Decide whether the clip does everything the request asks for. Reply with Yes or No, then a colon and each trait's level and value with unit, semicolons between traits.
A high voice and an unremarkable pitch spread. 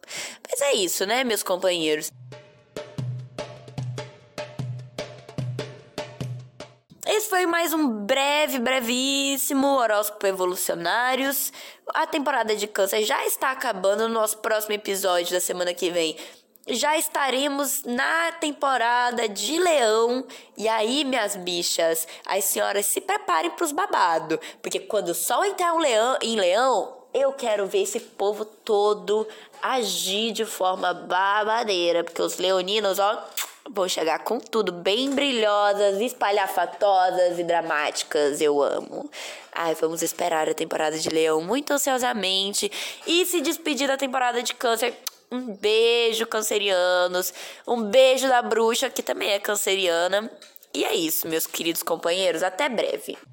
No: high, 215 Hz; wide, 7.1 semitones